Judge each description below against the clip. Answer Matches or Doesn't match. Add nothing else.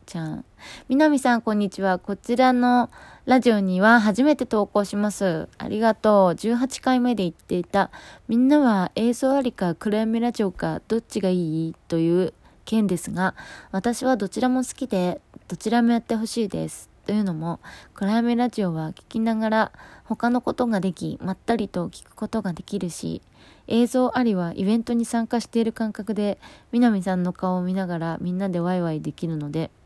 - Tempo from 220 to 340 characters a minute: Doesn't match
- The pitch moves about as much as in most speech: Matches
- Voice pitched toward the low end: Doesn't match